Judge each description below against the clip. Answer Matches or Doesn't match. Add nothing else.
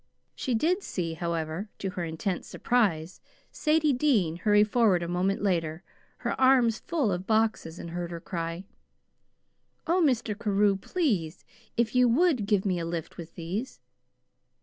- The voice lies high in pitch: Matches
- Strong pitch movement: Matches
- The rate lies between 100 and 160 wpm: Matches